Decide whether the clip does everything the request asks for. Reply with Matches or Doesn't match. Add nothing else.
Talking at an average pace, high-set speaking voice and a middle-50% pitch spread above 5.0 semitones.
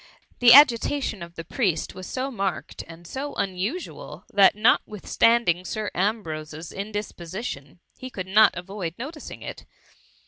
Doesn't match